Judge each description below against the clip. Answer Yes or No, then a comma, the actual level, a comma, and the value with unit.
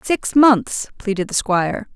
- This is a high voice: Yes, high, 225 Hz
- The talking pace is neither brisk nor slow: Yes, average, 155 wpm